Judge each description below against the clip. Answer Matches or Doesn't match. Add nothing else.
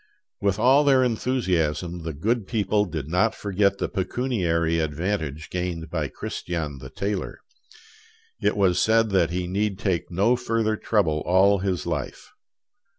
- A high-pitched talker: Doesn't match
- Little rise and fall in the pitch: Doesn't match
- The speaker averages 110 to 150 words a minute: Matches